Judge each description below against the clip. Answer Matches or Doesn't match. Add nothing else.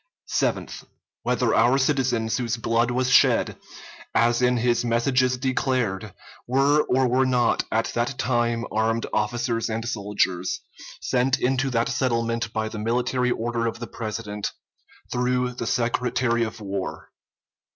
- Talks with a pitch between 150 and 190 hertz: Doesn't match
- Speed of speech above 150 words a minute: Doesn't match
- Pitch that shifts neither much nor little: Doesn't match